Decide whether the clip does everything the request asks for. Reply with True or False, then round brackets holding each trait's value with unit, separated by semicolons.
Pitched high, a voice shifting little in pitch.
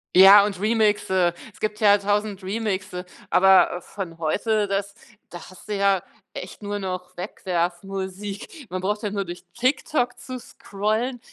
True (200 Hz; 2.2 semitones)